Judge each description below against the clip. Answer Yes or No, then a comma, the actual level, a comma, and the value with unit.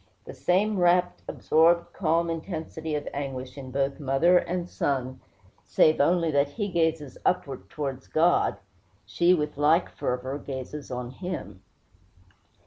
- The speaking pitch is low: No, medium, 155 Hz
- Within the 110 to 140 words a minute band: Yes, slow, 135 wpm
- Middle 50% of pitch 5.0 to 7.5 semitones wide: No, average, 4.2 semitones